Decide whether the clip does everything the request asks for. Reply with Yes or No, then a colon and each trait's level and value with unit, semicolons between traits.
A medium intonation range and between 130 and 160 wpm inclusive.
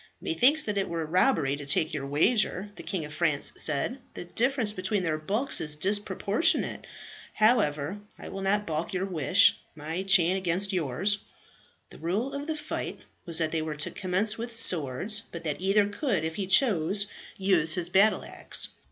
No: average, 4.7 semitones; average, 180 wpm